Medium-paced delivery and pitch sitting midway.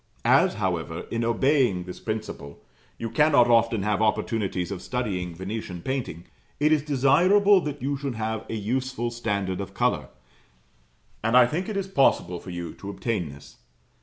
No: average, 165 wpm; low, 115 Hz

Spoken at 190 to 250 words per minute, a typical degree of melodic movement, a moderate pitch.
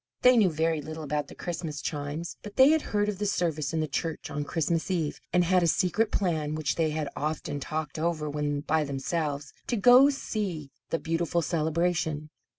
Yes: average, 200 wpm; average, 3.0 semitones; medium, 160 Hz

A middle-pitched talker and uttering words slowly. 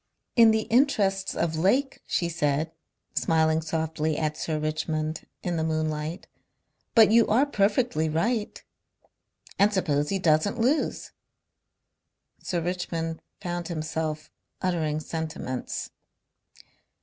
Yes: medium, 165 Hz; slow, 110 wpm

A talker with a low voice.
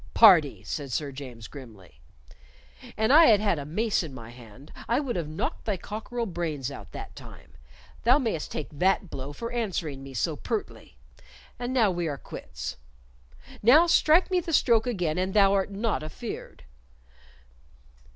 No: medium, 180 Hz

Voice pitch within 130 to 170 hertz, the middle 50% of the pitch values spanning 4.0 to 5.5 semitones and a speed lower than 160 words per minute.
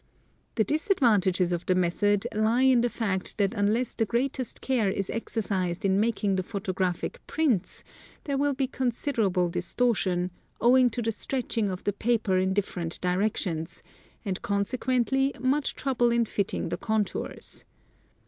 No: high, 215 Hz; average, 4.7 semitones; average, 150 wpm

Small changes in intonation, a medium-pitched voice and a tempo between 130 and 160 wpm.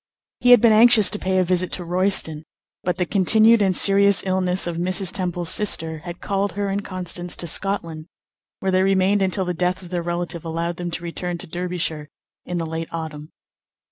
No: narrow, 2.3 semitones; medium, 180 Hz; average, 200 wpm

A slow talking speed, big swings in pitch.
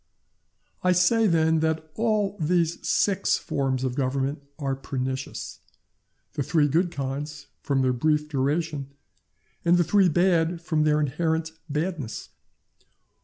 No: slow, 120 wpm; average, 3.9 semitones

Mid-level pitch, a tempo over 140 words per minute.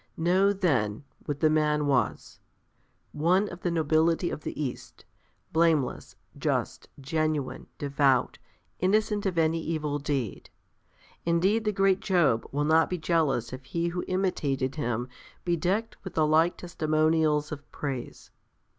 No: medium, 155 Hz; slow, 135 wpm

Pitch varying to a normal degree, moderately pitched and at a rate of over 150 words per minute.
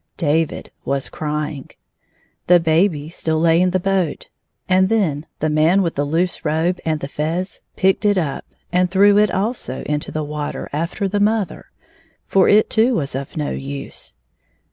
Yes: average, 4.2 semitones; medium, 165 Hz; average, 165 wpm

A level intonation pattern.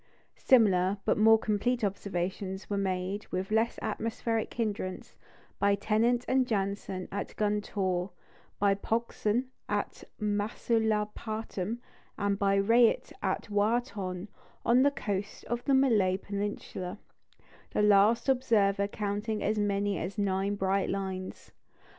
Yes: narrow, 2.3 semitones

